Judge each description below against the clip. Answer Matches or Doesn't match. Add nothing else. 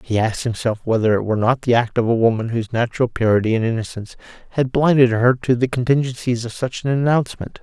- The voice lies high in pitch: Doesn't match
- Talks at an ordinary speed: Doesn't match